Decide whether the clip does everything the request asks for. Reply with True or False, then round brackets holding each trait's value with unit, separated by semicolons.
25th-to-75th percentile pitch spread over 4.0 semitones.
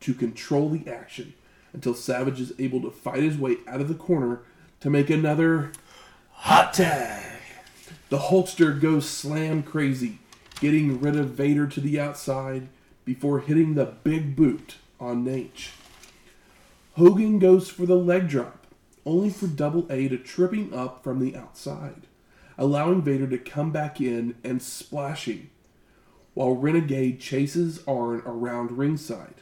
False (3.6 semitones)